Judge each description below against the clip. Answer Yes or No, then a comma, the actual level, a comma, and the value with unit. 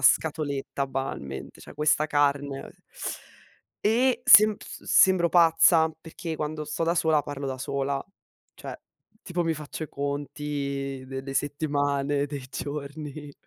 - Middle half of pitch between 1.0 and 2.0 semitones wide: No, narrow, 2.4 semitones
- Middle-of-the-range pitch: Yes, medium, 145 Hz